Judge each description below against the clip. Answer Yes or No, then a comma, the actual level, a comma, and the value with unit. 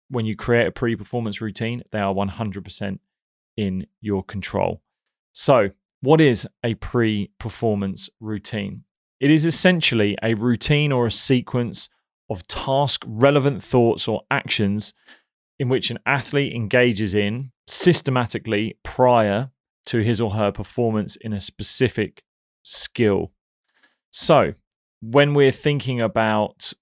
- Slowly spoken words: Yes, slow, 125 wpm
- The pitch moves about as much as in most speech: Yes, average, 3.7 semitones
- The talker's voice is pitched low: Yes, low, 115 Hz